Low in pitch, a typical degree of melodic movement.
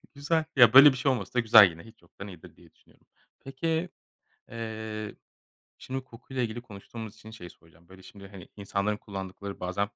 Yes: low, 110 Hz; average, 4.2 semitones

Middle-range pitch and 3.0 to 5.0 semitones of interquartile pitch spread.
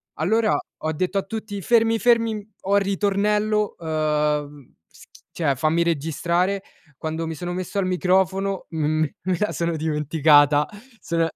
Yes: medium, 175 Hz; average, 4.2 semitones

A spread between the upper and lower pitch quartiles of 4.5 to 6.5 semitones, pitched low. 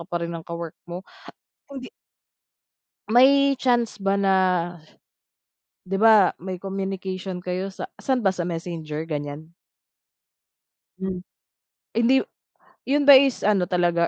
No: average, 4.8 semitones; high, 190 Hz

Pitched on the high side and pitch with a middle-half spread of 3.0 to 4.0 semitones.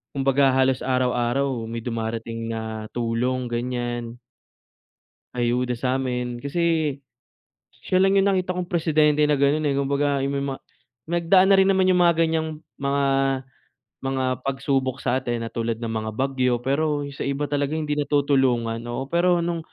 No: low, 135 Hz; average, 3.7 semitones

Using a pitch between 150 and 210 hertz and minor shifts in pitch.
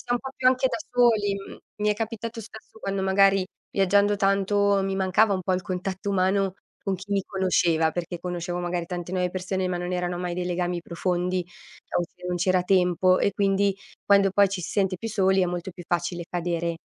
Yes: high, 190 Hz; narrow, 2.0 semitones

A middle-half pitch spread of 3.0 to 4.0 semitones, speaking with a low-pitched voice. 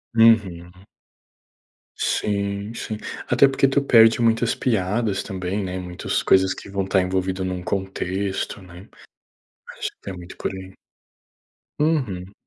Yes: average, 3.4 semitones; low, 100 Hz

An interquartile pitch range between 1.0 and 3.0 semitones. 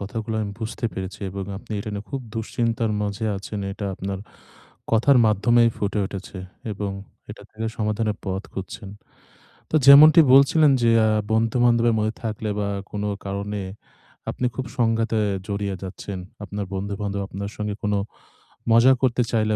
Yes: narrow, 2.4 semitones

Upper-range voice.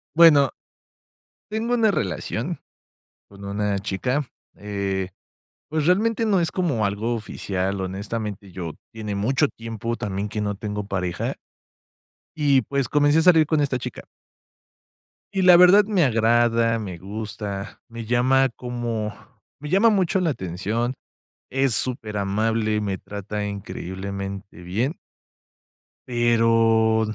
No: low, 115 Hz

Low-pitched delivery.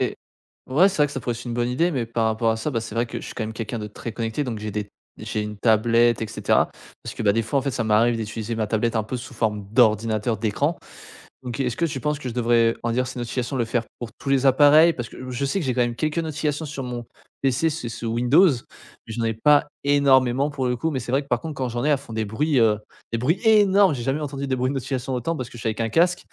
Yes: low, 120 Hz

